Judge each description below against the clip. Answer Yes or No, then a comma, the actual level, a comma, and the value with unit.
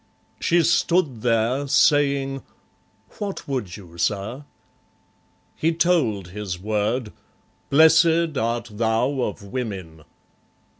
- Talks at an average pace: No, slow, 95 wpm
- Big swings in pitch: Yes, wide, 5.8 semitones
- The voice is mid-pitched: No, low, 125 Hz